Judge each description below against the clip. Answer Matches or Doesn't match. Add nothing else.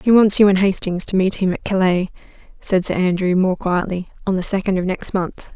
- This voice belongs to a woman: Matches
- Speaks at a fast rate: Matches